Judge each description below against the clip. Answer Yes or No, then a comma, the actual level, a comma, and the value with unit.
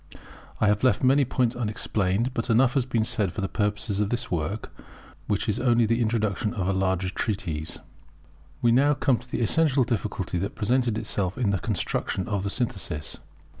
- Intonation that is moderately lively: Yes, average, 3.8 semitones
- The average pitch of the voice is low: Yes, low, 110 Hz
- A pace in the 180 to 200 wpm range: Yes, average, 185 wpm